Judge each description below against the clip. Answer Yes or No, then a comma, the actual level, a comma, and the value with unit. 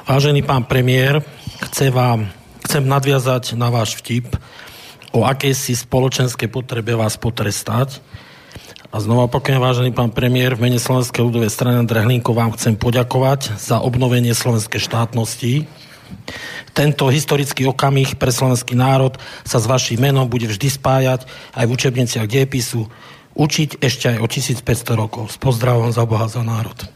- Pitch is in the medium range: No, low, 125 Hz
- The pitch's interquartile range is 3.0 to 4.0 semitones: No, narrow, 2.4 semitones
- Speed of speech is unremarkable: Yes, average, 145 wpm